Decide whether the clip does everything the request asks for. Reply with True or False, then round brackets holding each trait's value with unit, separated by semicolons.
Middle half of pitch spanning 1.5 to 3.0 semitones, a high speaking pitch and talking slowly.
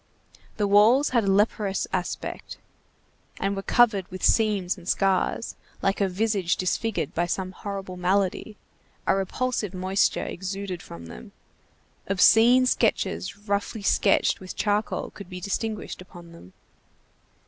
True (2.4 semitones; 195 Hz; 130 wpm)